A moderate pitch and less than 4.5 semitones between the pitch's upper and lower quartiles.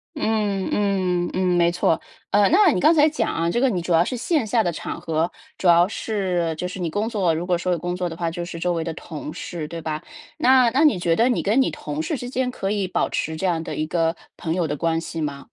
No: medium, 180 Hz; average, 5.0 semitones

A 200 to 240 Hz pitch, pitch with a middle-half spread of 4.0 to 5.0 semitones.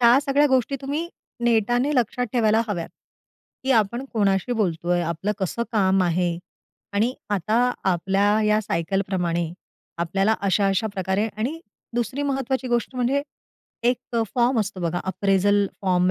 Yes: high, 210 Hz; average, 4.5 semitones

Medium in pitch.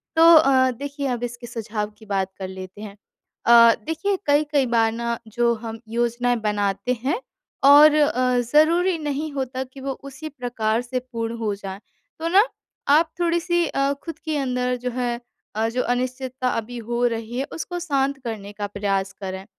No: high, 245 Hz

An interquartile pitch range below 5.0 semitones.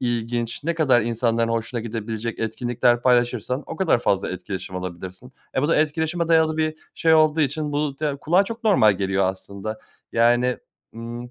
No: wide, 5.4 semitones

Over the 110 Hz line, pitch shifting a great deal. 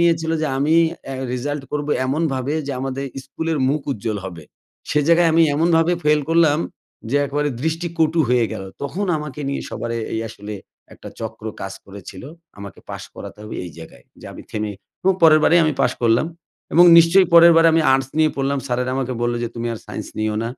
Yes: medium, 140 Hz; wide, 5.7 semitones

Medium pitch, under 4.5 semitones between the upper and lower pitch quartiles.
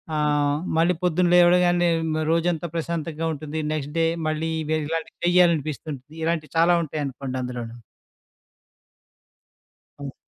Yes: medium, 155 Hz; narrow, 2.5 semitones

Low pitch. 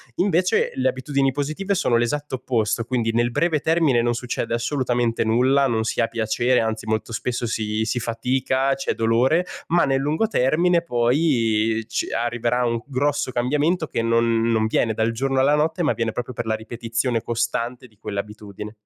Yes: low, 120 Hz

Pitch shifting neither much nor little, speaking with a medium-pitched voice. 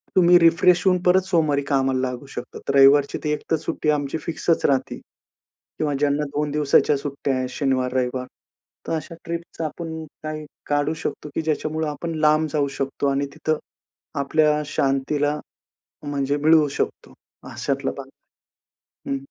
No: narrow, 2.2 semitones; medium, 150 Hz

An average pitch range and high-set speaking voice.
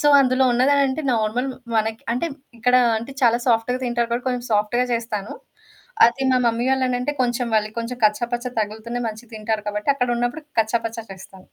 No: narrow, 2.2 semitones; high, 235 Hz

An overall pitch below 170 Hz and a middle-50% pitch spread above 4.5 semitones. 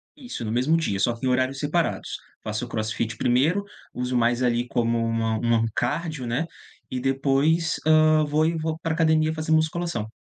Yes: low, 135 Hz; average, 5.1 semitones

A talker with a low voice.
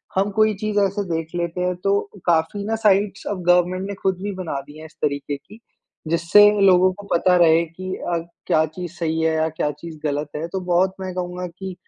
No: medium, 180 Hz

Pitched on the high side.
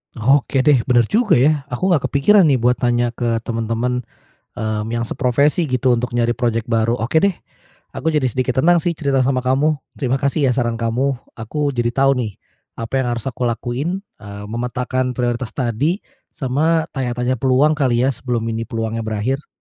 No: low, 125 Hz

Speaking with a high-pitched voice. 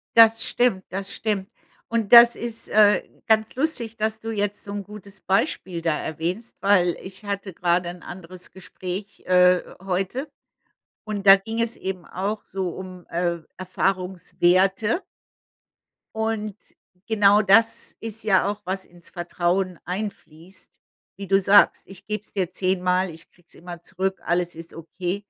Yes: high, 195 Hz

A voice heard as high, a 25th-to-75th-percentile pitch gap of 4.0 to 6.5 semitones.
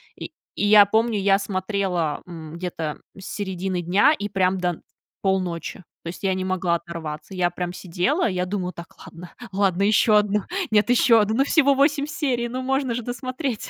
Yes: high, 195 Hz; average, 4.3 semitones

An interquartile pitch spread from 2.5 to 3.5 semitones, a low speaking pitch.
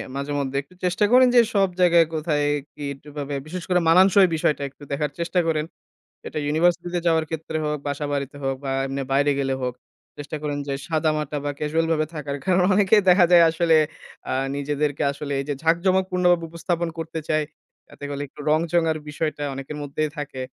No: average, 3.1 semitones; medium, 155 Hz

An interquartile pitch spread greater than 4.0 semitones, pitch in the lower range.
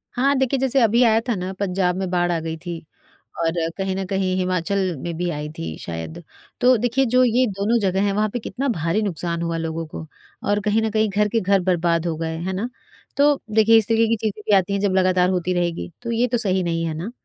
No: average, 4.4 semitones; high, 190 Hz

